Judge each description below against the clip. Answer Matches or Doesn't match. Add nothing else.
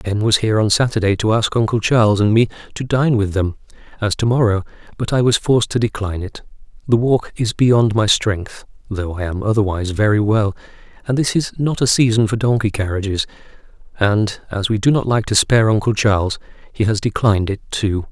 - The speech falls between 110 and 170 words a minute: Doesn't match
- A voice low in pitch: Matches